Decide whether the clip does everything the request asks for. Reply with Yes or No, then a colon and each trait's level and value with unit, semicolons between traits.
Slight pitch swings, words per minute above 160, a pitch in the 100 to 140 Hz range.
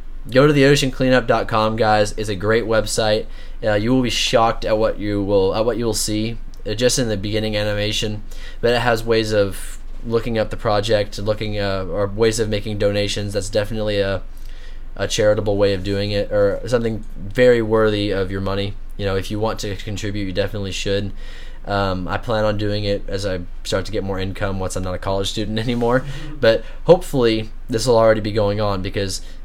Yes: narrow, 1.8 semitones; fast, 205 wpm; low, 105 Hz